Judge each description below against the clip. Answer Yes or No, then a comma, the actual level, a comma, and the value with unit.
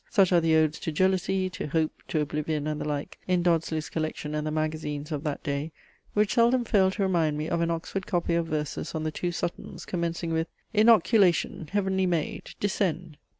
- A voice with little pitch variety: No, average, 3.5 semitones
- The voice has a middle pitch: Yes, medium, 165 Hz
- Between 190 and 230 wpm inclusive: Yes, average, 195 wpm